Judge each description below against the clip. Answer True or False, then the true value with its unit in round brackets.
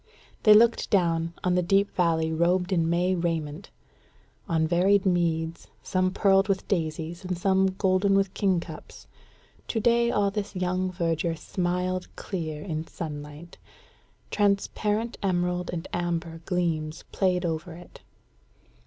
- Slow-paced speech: True (130 wpm)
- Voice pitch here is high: False (180 Hz)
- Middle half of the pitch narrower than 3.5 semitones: True (2.6 semitones)